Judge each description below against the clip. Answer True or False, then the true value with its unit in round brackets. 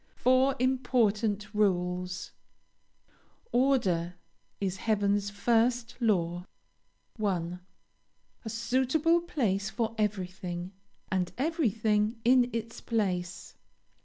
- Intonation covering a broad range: False (4.6 semitones)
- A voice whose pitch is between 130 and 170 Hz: False (215 Hz)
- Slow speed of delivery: True (80 wpm)